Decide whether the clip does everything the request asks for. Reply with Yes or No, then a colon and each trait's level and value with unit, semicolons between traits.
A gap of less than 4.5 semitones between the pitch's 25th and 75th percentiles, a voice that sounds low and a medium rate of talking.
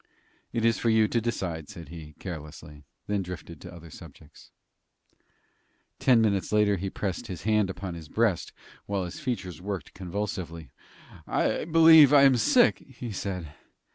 No: average, 5.1 semitones; very low, 95 Hz; average, 155 wpm